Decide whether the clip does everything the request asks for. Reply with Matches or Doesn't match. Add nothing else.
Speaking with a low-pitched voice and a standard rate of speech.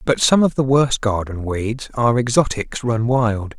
Matches